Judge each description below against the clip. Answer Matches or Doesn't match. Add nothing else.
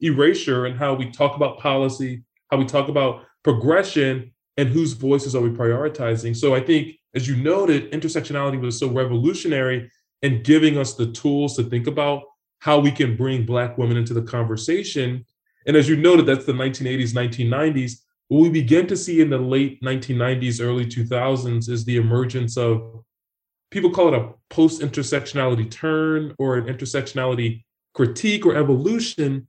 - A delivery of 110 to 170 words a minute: Matches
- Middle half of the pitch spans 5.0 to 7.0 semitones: Doesn't match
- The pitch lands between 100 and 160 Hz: Matches